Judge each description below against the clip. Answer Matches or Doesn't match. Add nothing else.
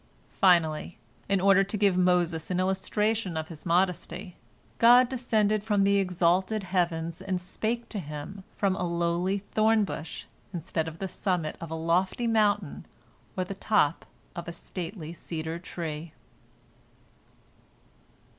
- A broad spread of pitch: Doesn't match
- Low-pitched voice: Doesn't match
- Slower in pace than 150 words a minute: Matches